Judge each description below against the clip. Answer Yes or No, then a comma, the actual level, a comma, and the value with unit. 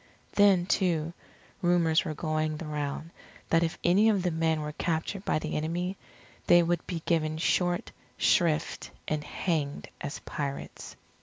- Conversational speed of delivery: Yes, average, 150 wpm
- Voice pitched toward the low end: No, medium, 165 Hz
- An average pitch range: No, narrow, 2.2 semitones